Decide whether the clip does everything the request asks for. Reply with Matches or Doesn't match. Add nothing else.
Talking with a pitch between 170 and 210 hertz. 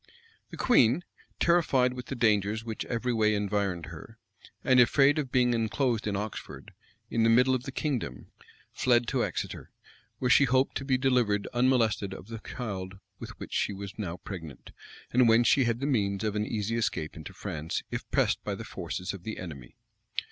Doesn't match